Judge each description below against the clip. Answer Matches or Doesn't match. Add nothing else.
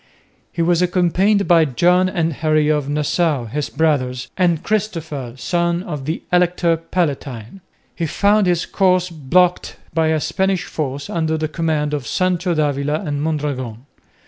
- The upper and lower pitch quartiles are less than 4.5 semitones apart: Matches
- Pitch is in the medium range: Matches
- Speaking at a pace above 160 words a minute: Doesn't match